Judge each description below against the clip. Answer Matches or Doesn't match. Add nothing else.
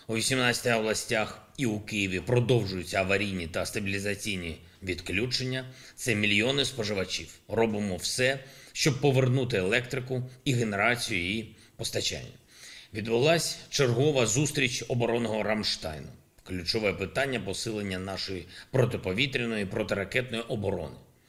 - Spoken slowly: Matches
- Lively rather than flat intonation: Doesn't match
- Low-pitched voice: Matches